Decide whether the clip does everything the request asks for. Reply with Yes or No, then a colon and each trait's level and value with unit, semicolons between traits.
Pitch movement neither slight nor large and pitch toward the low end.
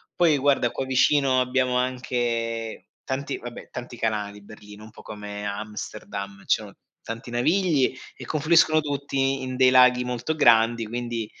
Yes: average, 3.1 semitones; low, 125 Hz